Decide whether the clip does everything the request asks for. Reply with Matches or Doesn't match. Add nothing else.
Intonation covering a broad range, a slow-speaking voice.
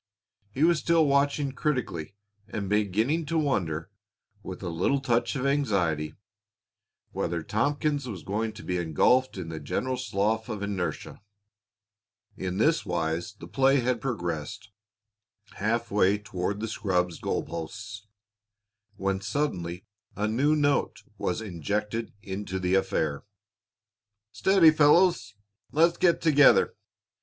Matches